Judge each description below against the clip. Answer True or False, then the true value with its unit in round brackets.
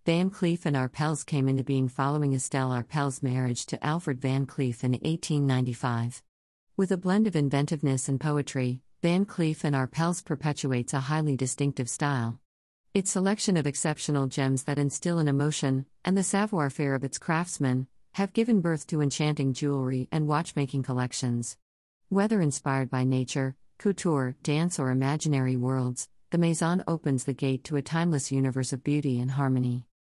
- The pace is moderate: True (160 wpm)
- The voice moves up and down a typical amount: True (3.4 semitones)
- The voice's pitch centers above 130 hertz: True (140 Hz)